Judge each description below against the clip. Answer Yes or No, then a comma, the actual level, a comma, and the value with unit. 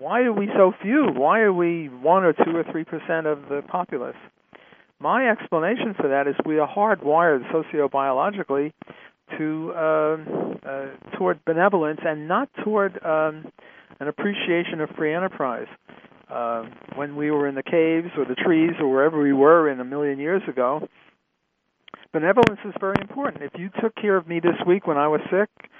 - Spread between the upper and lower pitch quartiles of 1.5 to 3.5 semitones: No, average, 4.6 semitones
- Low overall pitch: No, medium, 160 Hz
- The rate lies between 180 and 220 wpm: No, average, 170 wpm